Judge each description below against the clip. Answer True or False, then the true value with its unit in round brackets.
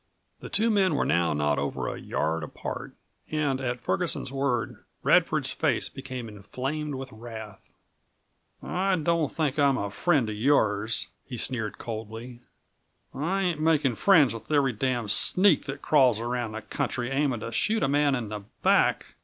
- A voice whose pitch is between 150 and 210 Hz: False (130 Hz)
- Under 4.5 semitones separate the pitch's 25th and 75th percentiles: False (5.1 semitones)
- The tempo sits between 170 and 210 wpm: False (160 wpm)